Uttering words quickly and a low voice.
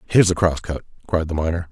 Yes: fast, 245 wpm; very low, 85 Hz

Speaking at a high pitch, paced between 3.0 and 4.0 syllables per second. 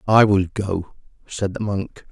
No: low, 100 Hz; 3.8 syllables/s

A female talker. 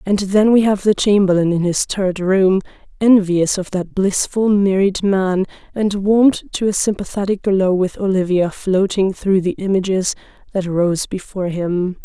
Yes: female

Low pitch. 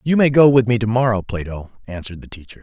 Yes: low, 115 Hz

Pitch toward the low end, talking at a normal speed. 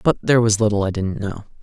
No: low, 105 Hz; fast, 260 wpm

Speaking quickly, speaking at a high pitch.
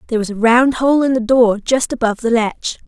Yes: fast, 250 wpm; high, 235 Hz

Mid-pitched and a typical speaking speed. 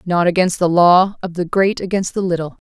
No: medium, 180 Hz; fast, 225 wpm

